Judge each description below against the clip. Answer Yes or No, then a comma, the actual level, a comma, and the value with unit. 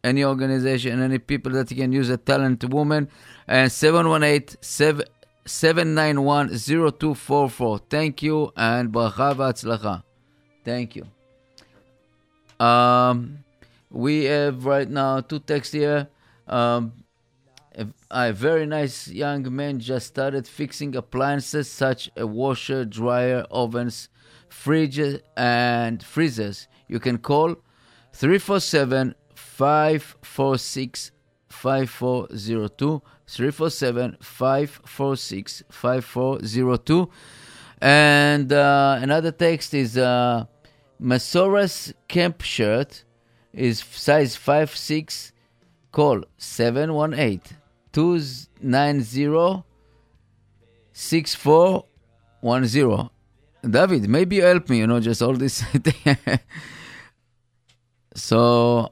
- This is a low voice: Yes, low, 130 Hz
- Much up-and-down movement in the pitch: No, average, 3.5 semitones